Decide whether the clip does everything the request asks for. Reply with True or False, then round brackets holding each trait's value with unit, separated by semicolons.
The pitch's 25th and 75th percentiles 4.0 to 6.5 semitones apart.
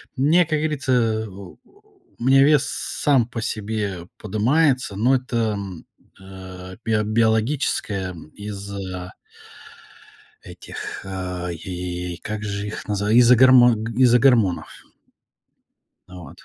True (4.6 semitones)